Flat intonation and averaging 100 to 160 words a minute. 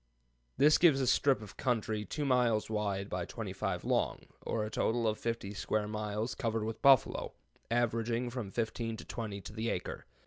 No: narrow, 2.3 semitones; average, 175 wpm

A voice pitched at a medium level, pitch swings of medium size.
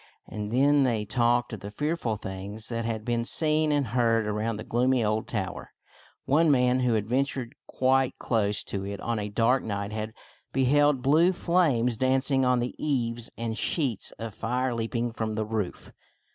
No: low, 120 Hz; average, 3.3 semitones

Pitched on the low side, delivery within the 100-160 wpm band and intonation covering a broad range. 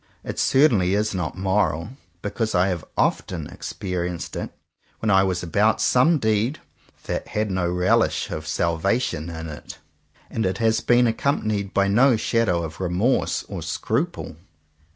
No: low, 100 Hz; average, 145 wpm; average, 4.2 semitones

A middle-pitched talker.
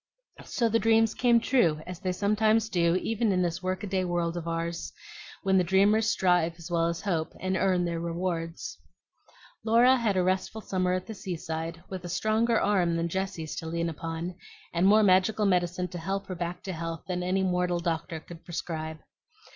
Yes: medium, 180 Hz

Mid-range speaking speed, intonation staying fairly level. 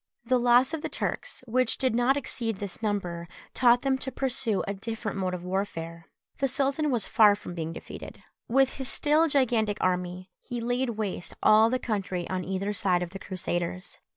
No: average, 185 wpm; wide, 5.6 semitones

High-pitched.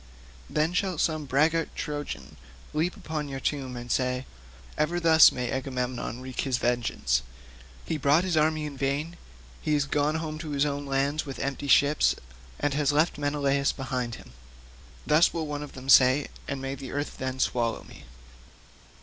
No: medium, 145 Hz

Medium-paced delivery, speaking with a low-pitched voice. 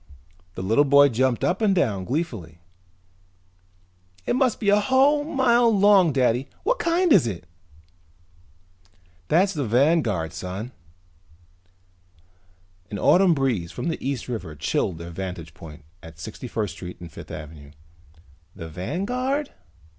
No: slow, 130 wpm; low, 130 Hz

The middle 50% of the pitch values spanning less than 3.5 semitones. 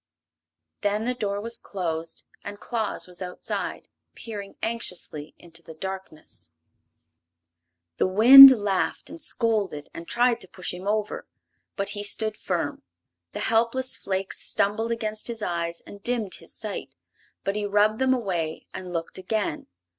No: average, 3.8 semitones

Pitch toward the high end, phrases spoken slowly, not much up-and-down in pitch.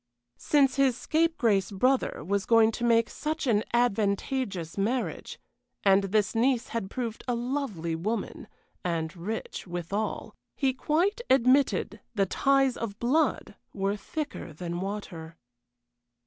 No: high, 225 Hz; slow, 125 wpm; average, 5.2 semitones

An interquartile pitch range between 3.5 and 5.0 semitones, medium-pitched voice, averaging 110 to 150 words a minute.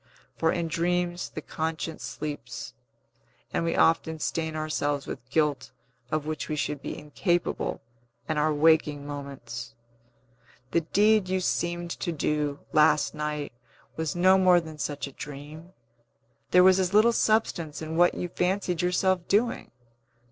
No: average, 3.0 semitones; medium, 160 Hz; average, 145 wpm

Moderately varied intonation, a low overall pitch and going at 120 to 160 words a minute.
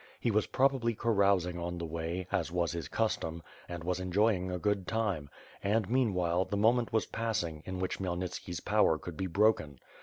No: average, 3.9 semitones; very low, 95 Hz; average, 185 wpm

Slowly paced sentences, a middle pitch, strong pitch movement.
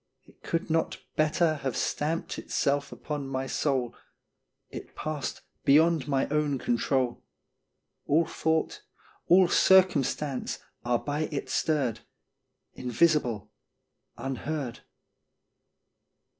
No: slow, 95 wpm; medium, 145 Hz; average, 3.0 semitones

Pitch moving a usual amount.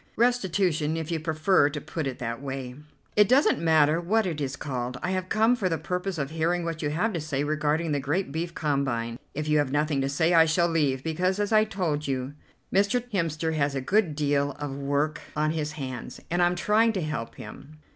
Yes: average, 3.9 semitones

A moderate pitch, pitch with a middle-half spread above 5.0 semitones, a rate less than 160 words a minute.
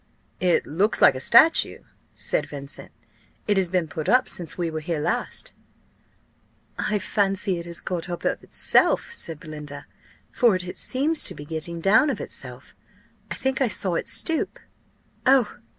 No: medium, 180 Hz; wide, 5.5 semitones; average, 165 wpm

